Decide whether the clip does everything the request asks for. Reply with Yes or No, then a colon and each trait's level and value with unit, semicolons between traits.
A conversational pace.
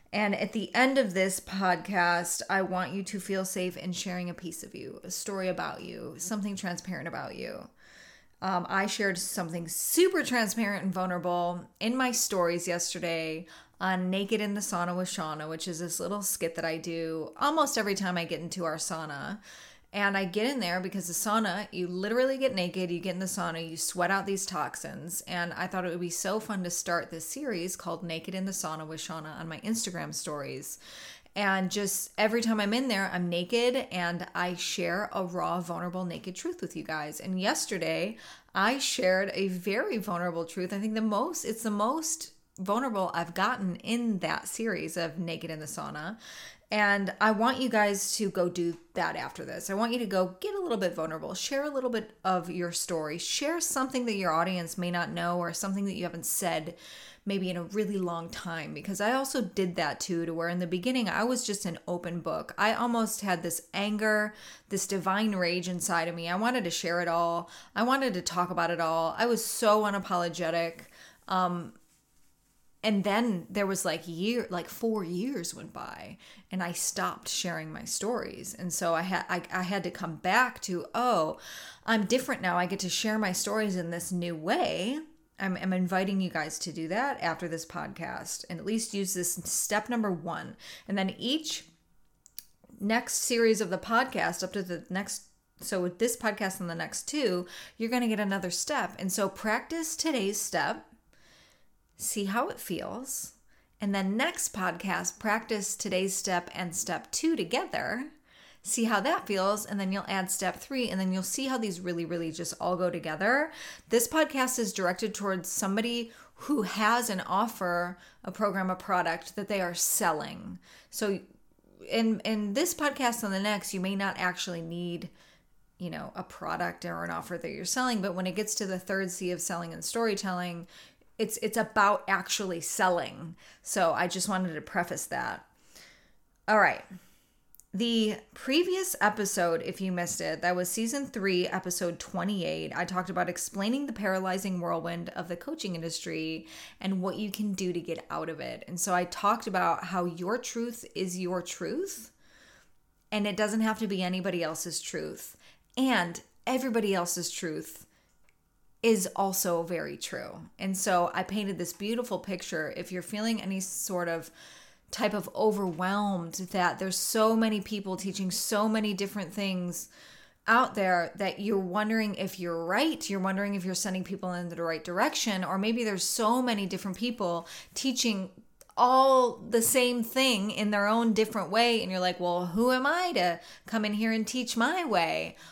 Yes: average, 190 wpm